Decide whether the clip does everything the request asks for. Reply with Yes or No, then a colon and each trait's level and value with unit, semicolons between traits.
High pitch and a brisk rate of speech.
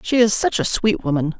Yes: high, 205 Hz; fast, 260 wpm